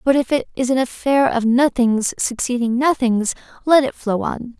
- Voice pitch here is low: No, very high, 250 Hz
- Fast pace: No, average, 185 wpm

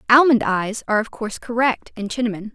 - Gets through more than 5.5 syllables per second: Yes, 6.1 syllables/s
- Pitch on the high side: Yes, high, 225 Hz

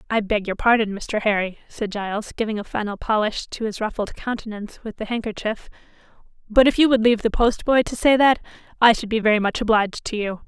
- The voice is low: No, high, 220 Hz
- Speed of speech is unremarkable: No, fast, 210 wpm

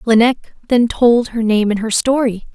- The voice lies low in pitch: No, high, 230 Hz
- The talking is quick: No, average, 190 wpm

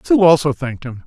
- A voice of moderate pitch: Yes, medium, 150 Hz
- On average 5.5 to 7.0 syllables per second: Yes, 6.3 syllables/s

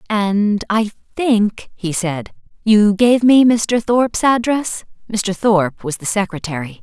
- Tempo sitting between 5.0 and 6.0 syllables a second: No, 3.8 syllables/s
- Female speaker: Yes, female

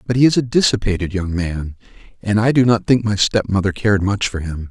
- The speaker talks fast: Yes, fast, 230 wpm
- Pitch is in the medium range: No, low, 105 Hz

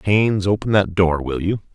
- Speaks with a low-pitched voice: Yes, very low, 95 Hz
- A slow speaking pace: No, fast, 205 wpm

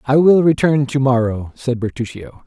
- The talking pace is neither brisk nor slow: Yes, average, 170 wpm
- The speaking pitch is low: Yes, low, 130 Hz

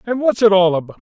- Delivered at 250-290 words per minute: Yes, fast, 280 wpm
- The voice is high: Yes, high, 200 Hz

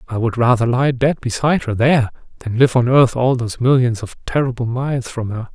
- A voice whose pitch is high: No, low, 125 Hz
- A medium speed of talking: No, fast, 215 wpm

